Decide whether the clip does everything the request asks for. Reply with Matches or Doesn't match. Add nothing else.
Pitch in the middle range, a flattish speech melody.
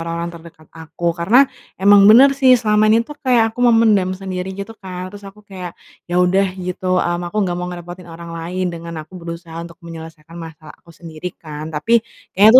Doesn't match